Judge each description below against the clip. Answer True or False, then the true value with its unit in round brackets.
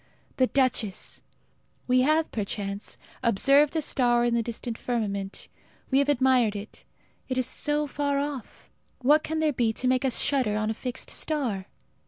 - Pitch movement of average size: True (4.1 semitones)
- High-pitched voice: True (255 Hz)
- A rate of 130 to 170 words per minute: True (165 wpm)